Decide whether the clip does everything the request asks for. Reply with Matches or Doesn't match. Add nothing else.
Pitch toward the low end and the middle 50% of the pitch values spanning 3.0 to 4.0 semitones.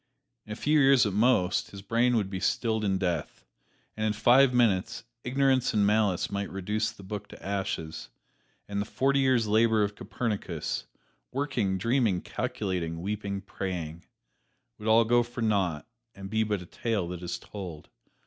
Matches